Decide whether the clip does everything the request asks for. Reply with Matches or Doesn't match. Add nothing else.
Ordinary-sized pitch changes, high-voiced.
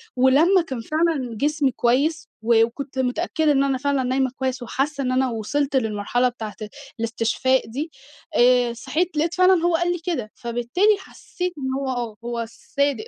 Matches